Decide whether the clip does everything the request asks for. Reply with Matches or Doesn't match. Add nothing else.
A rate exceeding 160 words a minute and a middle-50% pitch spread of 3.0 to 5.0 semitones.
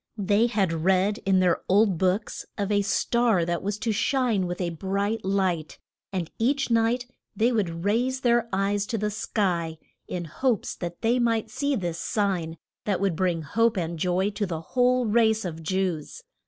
Matches